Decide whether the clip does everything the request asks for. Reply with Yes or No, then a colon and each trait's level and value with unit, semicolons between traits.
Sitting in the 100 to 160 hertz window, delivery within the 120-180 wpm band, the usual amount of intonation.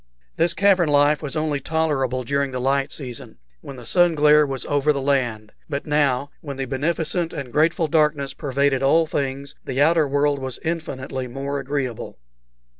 No: medium, 140 Hz; average, 170 wpm; narrow, 2.3 semitones